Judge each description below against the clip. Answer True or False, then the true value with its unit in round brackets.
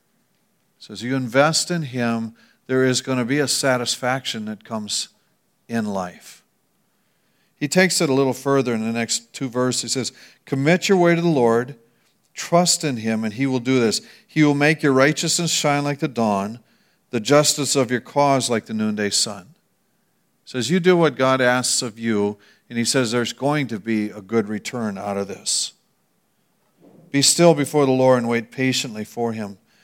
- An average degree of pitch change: True (4.0 semitones)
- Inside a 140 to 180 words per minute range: False (190 wpm)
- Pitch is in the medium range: False (130 Hz)